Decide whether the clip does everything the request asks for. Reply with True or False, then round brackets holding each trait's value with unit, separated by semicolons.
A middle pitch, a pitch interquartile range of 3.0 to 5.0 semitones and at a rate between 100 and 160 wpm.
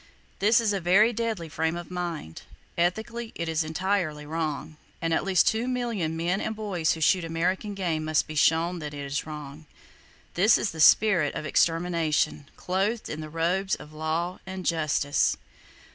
False (170 Hz; 3.7 semitones; 175 wpm)